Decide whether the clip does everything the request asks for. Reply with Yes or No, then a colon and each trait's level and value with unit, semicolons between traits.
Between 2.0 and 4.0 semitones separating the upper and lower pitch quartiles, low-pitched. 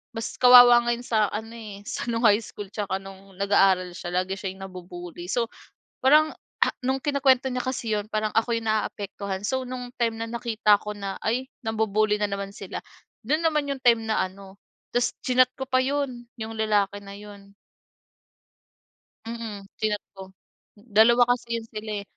No: average, 3.4 semitones; high, 220 Hz